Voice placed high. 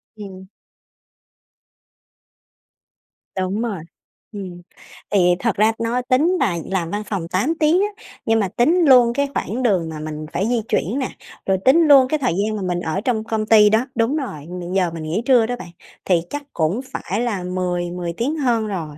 Yes: high, 210 Hz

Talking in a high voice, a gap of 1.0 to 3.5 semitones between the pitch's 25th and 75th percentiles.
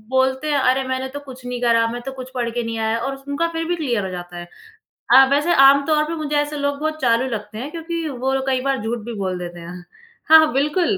No: very high, 265 Hz; average, 4.1 semitones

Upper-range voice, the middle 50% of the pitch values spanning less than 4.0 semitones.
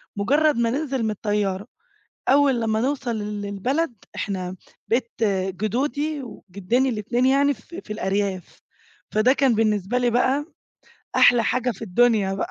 No: high, 230 Hz; average, 4.3 semitones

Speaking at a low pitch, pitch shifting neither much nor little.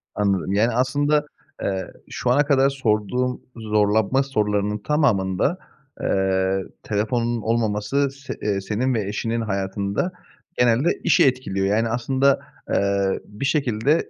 Yes: low, 110 Hz; average, 4.7 semitones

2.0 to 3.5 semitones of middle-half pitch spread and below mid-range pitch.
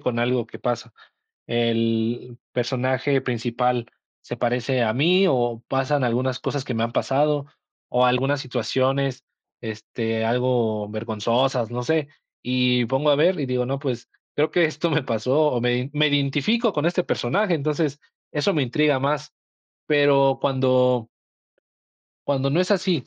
Yes: average, 3.2 semitones; low, 130 Hz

